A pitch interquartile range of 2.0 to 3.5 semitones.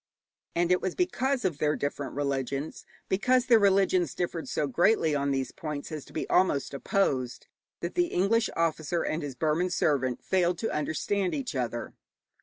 No: average, 5.2 semitones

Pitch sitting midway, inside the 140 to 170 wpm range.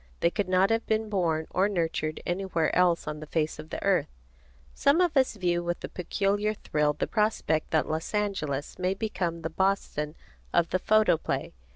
No: medium, 180 Hz; average, 185 wpm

